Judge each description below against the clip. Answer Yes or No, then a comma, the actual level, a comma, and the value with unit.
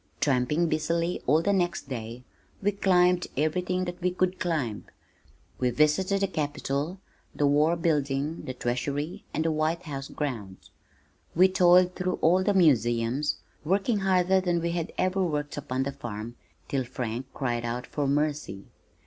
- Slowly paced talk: No, average, 155 wpm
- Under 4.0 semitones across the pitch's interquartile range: No, average, 5.1 semitones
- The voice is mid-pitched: Yes, medium, 155 Hz